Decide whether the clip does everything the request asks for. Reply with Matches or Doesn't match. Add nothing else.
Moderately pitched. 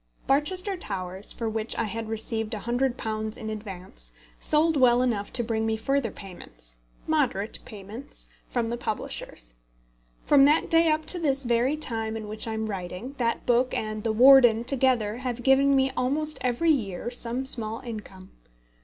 Doesn't match